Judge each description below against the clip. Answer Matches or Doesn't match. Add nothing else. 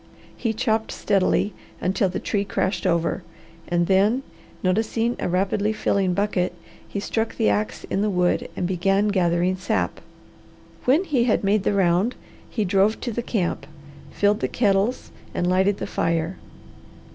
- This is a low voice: Doesn't match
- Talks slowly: Doesn't match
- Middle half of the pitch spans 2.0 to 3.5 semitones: Matches